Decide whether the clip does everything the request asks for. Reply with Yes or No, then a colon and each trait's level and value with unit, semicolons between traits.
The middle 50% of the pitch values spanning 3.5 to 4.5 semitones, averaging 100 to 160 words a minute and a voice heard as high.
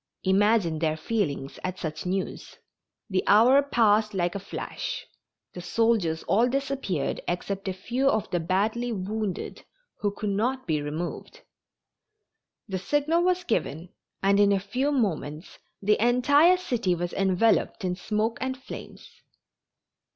No: average, 5.2 semitones; slow, 135 wpm; high, 205 Hz